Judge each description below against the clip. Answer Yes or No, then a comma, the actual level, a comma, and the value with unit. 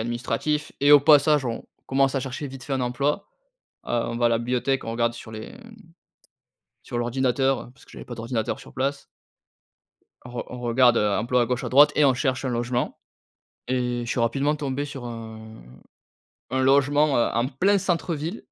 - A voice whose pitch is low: Yes, low, 130 Hz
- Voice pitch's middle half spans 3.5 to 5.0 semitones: No, average, 3.0 semitones